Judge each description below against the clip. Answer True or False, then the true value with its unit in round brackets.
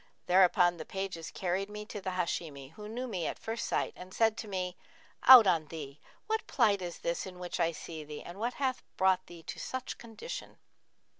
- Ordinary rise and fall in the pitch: True (4.3 semitones)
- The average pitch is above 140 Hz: True (185 Hz)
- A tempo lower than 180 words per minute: False (205 wpm)